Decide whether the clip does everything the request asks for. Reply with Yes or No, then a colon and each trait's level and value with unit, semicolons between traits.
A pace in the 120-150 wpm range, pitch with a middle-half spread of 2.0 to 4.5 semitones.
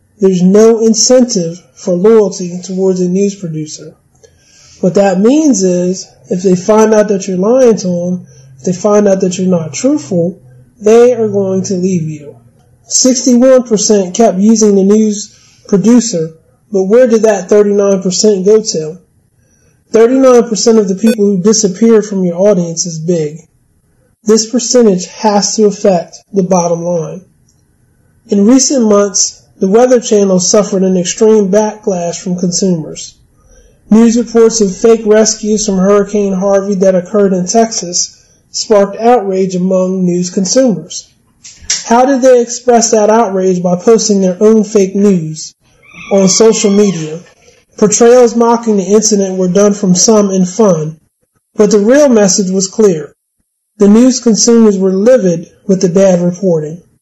Yes: average, 145 wpm; average, 3.3 semitones